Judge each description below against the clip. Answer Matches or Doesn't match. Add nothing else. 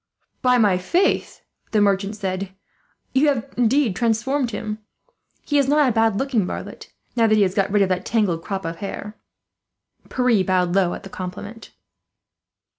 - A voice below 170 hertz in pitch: Doesn't match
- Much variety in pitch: Doesn't match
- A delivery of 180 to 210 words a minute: Doesn't match